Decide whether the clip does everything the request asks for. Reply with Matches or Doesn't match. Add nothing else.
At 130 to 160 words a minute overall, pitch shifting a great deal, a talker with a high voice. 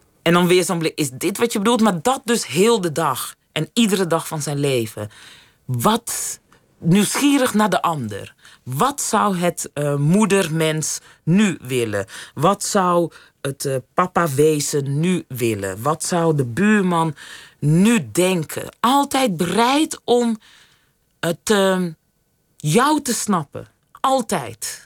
Doesn't match